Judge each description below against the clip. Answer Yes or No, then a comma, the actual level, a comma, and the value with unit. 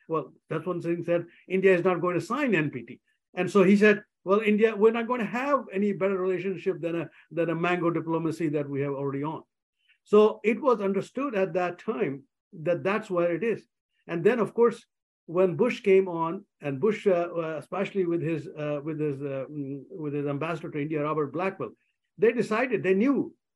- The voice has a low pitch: No, medium, 180 Hz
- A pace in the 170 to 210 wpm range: Yes, average, 200 wpm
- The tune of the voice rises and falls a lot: No, average, 4.2 semitones